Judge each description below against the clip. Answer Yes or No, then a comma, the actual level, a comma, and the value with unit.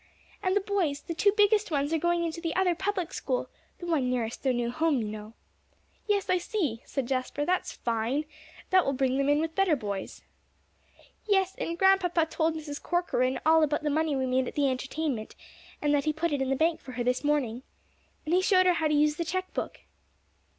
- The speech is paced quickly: Yes, fast, 215 wpm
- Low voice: No, very high, 310 Hz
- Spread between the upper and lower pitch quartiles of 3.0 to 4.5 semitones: No, average, 4.9 semitones